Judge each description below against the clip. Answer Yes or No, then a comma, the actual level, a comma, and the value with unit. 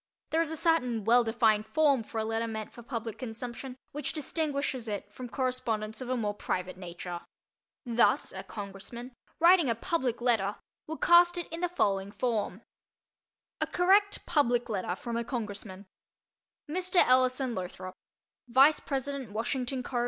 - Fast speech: No, average, 155 wpm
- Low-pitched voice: No, high, 240 Hz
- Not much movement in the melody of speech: No, average, 4.5 semitones